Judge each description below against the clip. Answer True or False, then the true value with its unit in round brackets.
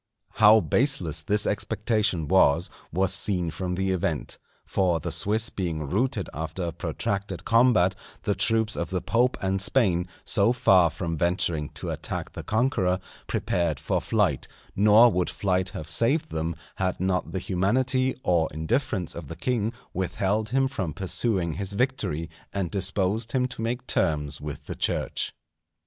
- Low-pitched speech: True (95 Hz)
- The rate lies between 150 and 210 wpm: True (155 wpm)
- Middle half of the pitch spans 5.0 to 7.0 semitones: False (4.6 semitones)